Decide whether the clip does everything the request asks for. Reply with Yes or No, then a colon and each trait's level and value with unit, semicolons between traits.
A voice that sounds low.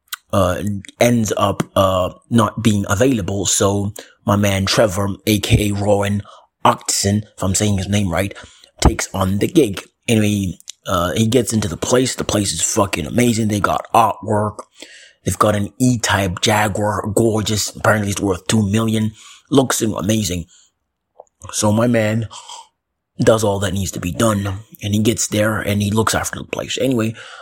Yes: low, 105 Hz